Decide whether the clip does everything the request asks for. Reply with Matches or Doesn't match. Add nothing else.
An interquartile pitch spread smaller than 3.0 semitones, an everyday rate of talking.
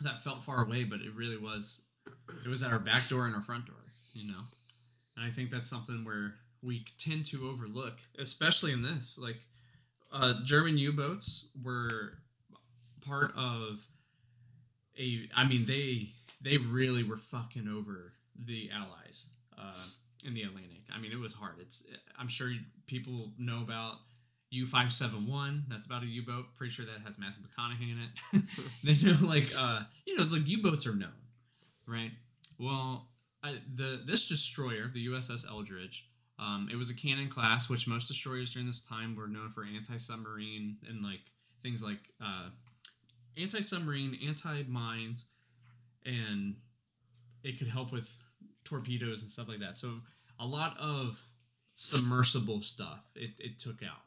Matches